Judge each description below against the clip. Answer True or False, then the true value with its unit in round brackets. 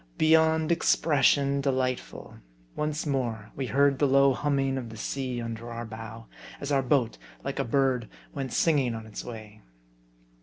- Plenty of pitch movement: False (3.4 semitones)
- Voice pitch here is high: False (135 Hz)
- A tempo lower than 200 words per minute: True (155 wpm)